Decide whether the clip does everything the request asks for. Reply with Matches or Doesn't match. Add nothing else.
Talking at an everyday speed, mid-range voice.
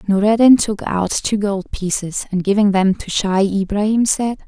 Doesn't match